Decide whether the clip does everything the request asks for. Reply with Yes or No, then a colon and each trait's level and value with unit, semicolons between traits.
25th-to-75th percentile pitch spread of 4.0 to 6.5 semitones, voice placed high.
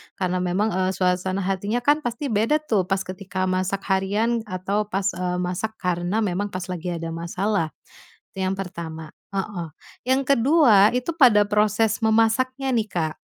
No: average, 3.5 semitones; high, 195 Hz